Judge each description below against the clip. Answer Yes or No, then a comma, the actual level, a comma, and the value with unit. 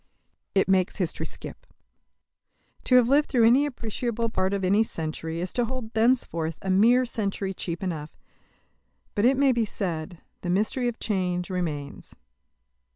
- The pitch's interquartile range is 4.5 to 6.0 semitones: Yes, average, 4.9 semitones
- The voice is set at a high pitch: Yes, high, 200 Hz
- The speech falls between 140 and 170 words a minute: Yes, average, 155 wpm